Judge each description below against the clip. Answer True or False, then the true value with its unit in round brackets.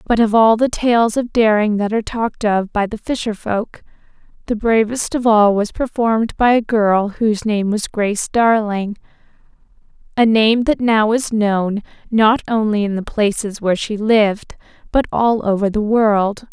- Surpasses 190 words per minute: False (170 wpm)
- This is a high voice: True (215 Hz)